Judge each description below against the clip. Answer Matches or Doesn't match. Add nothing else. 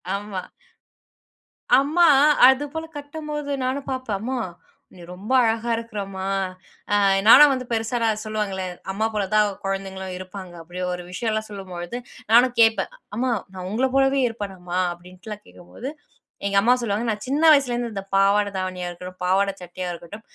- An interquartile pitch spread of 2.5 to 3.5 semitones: Doesn't match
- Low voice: Doesn't match